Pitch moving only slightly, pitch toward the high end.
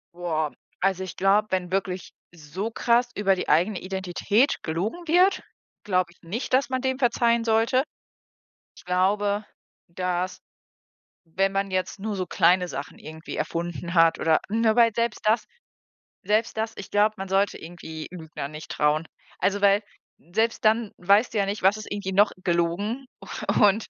No: average, 3.8 semitones; high, 195 Hz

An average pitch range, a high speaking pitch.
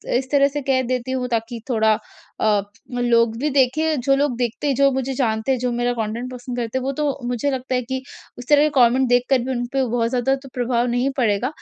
No: narrow, 2.0 semitones; very high, 250 Hz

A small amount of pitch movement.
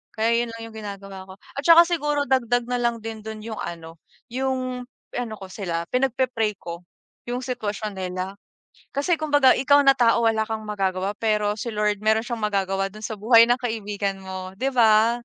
No: average, 3.7 semitones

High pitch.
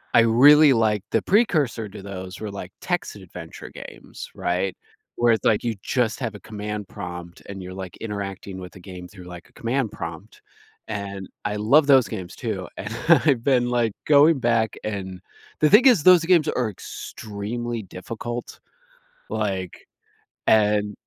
No: low, 105 Hz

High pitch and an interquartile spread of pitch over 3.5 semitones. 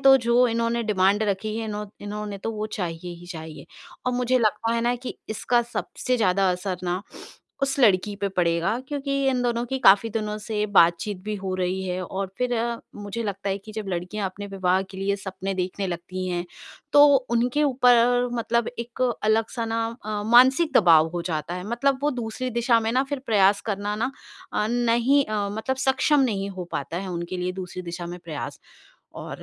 Yes: high, 210 Hz; average, 4.2 semitones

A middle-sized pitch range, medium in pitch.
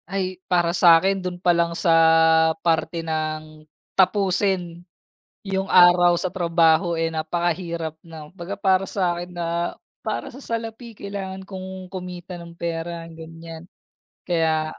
No: narrow, 2.3 semitones; medium, 175 Hz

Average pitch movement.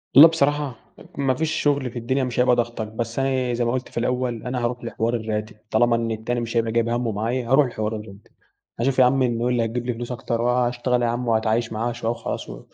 No: narrow, 1.6 semitones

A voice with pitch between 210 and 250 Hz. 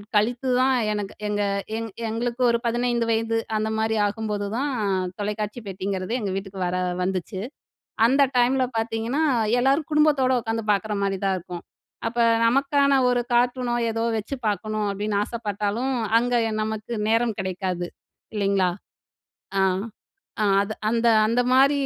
Yes: high, 225 Hz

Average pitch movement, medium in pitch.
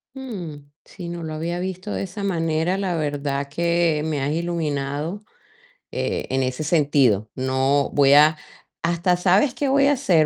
Yes: average, 3.9 semitones; medium, 160 Hz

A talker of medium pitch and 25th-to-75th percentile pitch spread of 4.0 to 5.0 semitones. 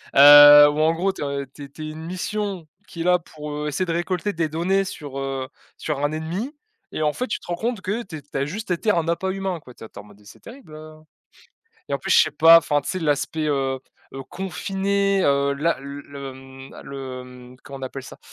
Yes: medium, 155 Hz; average, 4.7 semitones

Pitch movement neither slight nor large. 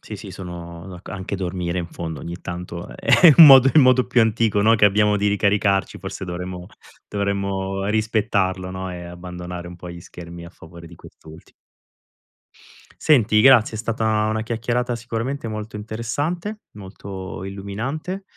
Yes: average, 4.1 semitones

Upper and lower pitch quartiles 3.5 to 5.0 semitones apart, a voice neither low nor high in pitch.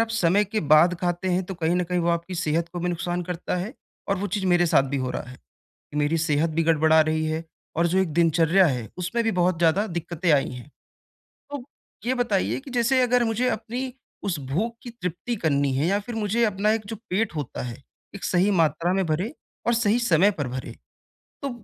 Yes: average, 4.7 semitones; medium, 180 Hz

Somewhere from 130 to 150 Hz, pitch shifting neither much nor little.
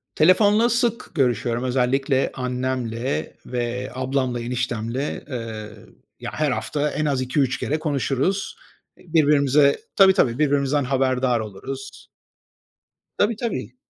Yes: low, 135 Hz; average, 3.3 semitones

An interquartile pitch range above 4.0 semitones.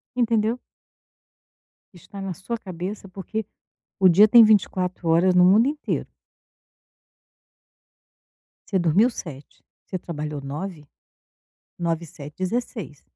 Yes: average, 4.4 semitones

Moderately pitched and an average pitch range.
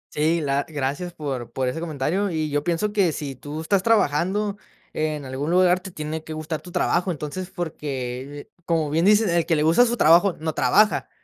Yes: medium, 160 Hz; average, 3.7 semitones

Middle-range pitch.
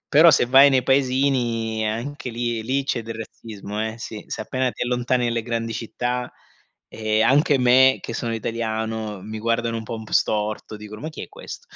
No: low, 115 Hz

